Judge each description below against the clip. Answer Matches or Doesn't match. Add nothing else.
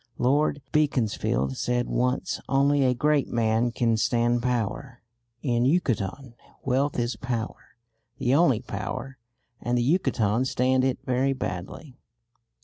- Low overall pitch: Matches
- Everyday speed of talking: Doesn't match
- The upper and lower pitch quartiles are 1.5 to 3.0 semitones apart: Matches